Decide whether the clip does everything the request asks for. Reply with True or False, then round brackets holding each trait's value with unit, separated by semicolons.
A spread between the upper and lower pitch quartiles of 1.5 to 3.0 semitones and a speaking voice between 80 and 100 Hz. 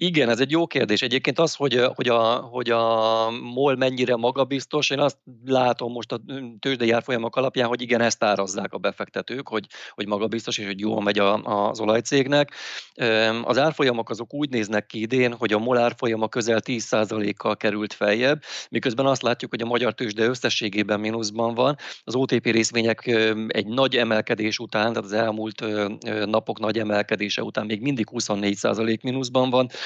False (2.6 semitones; 115 Hz)